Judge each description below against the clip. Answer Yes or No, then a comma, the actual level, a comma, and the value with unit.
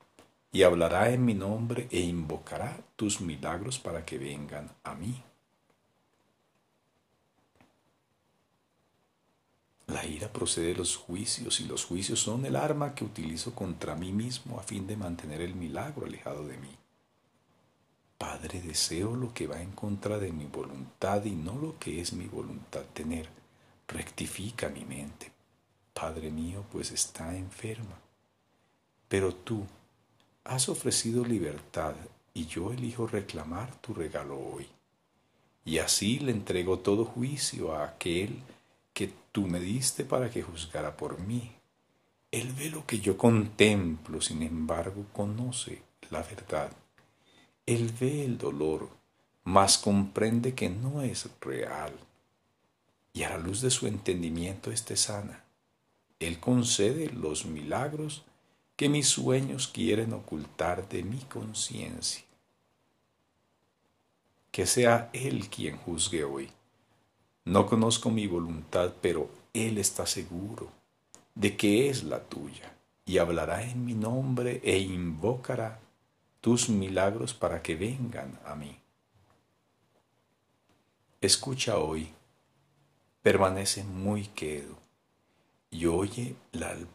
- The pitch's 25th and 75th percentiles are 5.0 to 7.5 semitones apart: Yes, wide, 5.6 semitones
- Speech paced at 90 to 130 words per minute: Yes, slow, 125 wpm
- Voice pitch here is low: Yes, low, 105 Hz